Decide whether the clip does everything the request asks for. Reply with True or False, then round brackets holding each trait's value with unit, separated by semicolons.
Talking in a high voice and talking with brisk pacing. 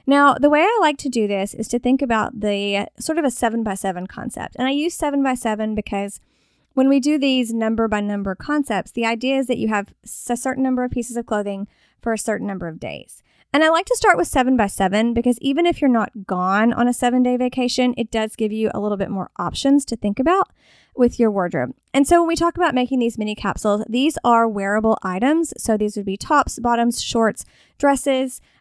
True (235 Hz; 235 wpm)